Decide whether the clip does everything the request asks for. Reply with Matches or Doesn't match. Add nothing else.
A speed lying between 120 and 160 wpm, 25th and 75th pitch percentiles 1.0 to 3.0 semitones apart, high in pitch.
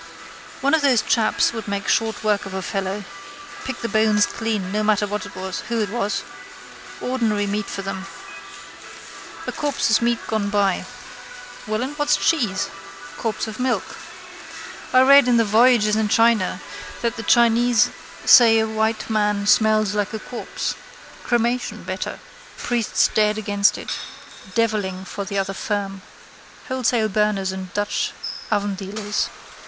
Matches